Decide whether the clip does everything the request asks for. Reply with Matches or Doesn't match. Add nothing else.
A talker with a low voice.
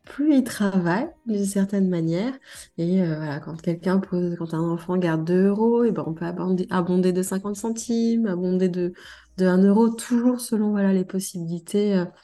Doesn't match